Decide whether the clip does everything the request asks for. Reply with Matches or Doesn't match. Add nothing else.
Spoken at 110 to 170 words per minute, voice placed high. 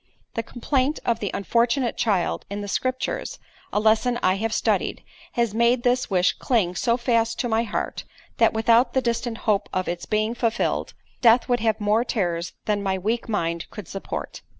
Doesn't match